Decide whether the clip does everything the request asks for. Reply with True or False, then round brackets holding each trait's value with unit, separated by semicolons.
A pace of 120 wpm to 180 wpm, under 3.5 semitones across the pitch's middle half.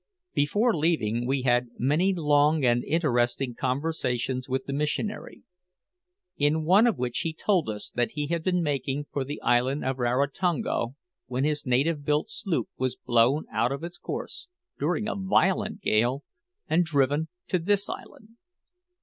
False (155 wpm; 4.8 semitones)